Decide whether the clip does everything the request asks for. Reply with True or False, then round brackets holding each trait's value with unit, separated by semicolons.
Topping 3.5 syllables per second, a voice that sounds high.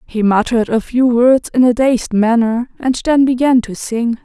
True (4.6 syllables/s; 240 Hz)